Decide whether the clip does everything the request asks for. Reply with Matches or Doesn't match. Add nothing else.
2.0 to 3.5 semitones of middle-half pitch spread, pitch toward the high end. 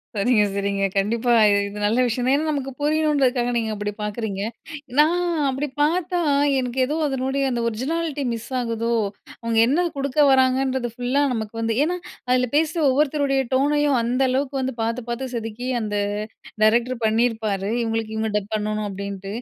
Doesn't match